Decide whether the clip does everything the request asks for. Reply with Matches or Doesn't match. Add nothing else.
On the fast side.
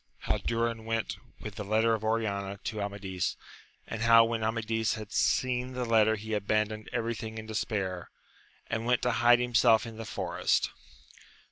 Doesn't match